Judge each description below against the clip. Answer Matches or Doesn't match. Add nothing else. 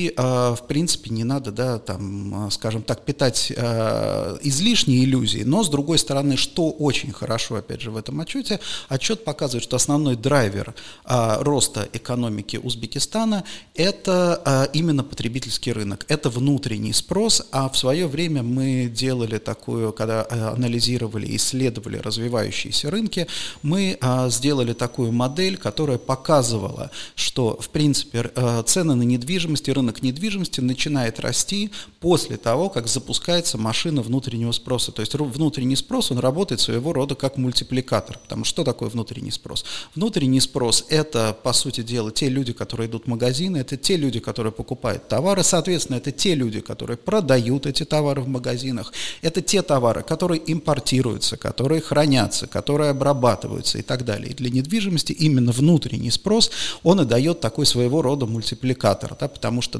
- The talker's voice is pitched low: Matches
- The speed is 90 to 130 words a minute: Doesn't match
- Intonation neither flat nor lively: Matches